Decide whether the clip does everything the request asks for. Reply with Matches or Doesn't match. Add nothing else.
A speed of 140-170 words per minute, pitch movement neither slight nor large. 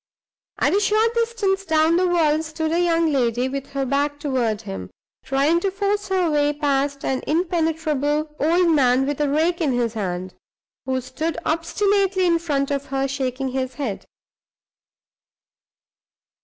Matches